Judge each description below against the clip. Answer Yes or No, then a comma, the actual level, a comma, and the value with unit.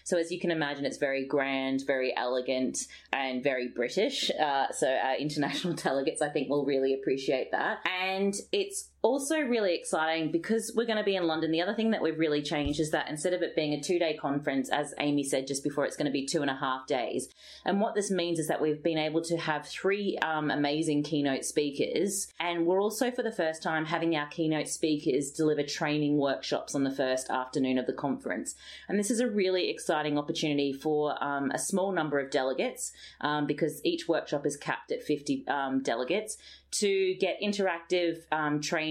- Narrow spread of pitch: No, average, 3.6 semitones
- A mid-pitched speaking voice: Yes, medium, 155 Hz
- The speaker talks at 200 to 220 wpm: Yes, fast, 205 wpm